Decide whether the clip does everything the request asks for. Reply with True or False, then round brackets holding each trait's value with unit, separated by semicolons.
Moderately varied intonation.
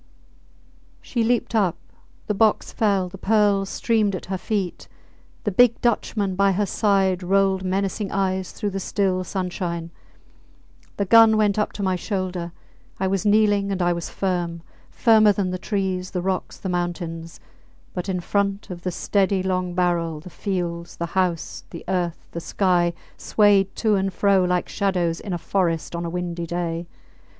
False (2.3 semitones)